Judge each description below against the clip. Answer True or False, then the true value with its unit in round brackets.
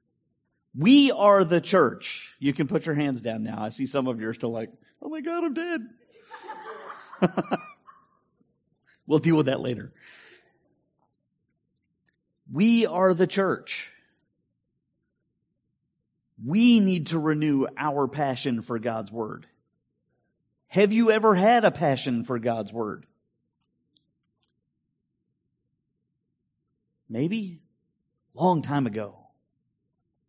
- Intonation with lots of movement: True (8.7 semitones)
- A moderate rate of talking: False (105 wpm)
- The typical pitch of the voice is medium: True (155 Hz)